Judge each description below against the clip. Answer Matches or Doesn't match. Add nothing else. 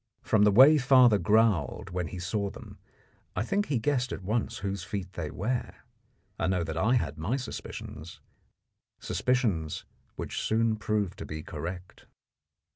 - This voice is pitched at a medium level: Doesn't match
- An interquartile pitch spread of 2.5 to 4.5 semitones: Doesn't match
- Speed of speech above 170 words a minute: Doesn't match